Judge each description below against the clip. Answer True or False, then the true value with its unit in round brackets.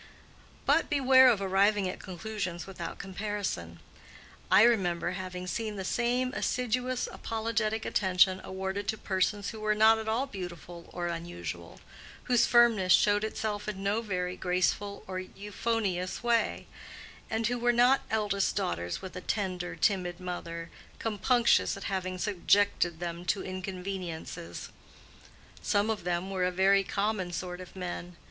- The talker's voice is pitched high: True (195 Hz)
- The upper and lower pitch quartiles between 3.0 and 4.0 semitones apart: True (3.4 semitones)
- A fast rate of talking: False (140 wpm)